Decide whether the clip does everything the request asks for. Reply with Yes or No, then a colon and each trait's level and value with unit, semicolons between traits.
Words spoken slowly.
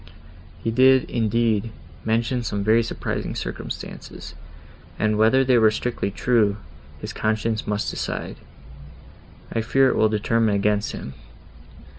Yes: slow, 125 wpm